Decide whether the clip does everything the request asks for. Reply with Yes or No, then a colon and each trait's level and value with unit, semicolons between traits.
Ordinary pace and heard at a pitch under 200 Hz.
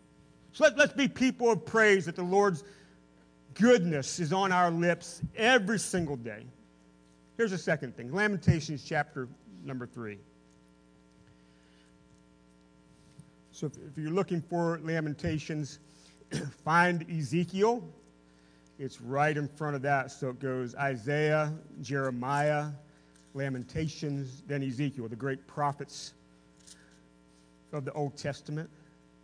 No: slow, 115 wpm; medium, 140 Hz